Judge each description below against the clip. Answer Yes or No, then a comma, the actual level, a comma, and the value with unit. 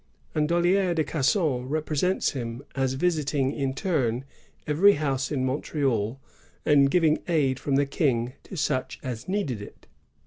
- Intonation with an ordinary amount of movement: Yes, average, 3.7 semitones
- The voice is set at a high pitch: No, medium, 140 Hz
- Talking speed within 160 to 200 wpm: No, average, 145 wpm